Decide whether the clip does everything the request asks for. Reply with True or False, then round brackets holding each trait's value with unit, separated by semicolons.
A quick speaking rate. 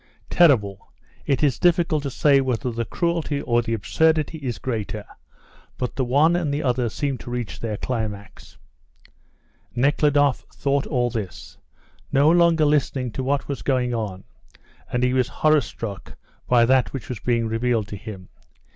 False (160 wpm)